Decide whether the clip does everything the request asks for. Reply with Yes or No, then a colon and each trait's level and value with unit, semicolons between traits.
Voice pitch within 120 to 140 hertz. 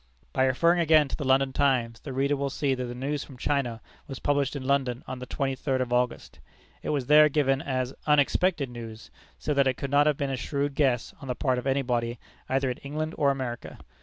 Yes: low, 135 Hz